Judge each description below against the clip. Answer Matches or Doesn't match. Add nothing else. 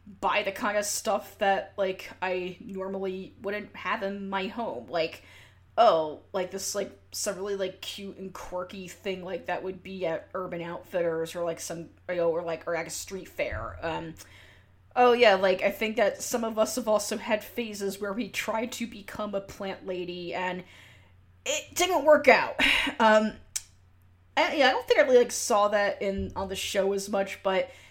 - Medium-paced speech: Matches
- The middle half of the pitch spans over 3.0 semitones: Matches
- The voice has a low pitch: Doesn't match